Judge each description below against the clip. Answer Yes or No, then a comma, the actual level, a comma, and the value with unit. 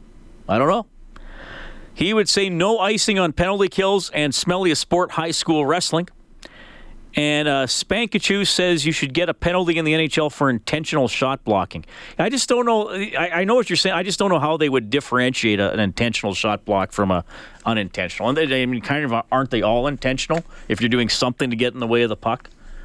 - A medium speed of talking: No, fast, 220 wpm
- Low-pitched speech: No, medium, 155 Hz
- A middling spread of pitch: No, wide, 6.6 semitones